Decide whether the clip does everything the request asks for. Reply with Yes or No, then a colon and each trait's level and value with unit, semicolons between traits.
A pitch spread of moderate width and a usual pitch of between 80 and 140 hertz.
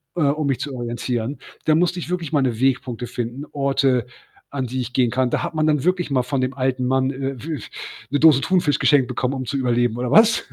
Yes: average, 3.0 semitones; low, 135 Hz